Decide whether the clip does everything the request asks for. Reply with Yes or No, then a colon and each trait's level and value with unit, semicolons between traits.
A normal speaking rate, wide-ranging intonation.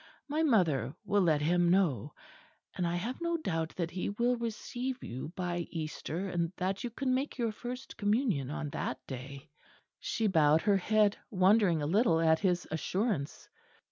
Yes: average, 170 wpm; wide, 5.9 semitones